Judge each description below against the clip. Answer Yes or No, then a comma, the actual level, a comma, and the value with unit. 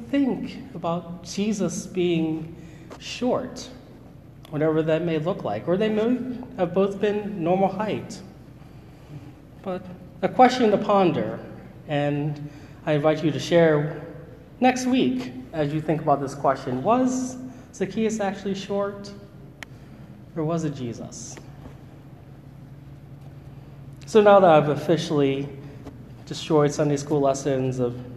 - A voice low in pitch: No, medium, 155 Hz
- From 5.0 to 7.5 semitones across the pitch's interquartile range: Yes, wide, 5.5 semitones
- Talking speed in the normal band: No, slow, 115 wpm